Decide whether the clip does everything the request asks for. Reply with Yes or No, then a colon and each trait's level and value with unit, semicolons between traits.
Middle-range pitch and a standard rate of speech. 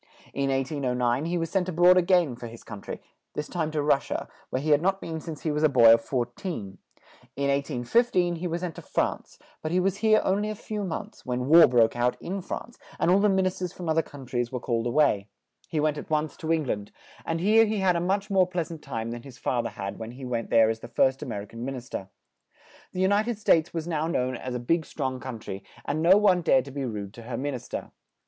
No: medium, 150 Hz; fast, 270 wpm